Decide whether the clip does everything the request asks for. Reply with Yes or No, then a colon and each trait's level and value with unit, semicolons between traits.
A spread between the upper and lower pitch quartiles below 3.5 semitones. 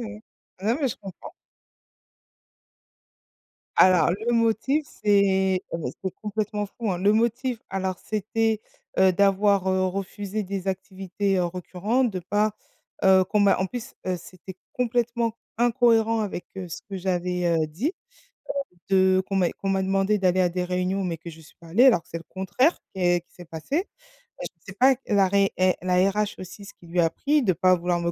Yes: average, 2.9 semitones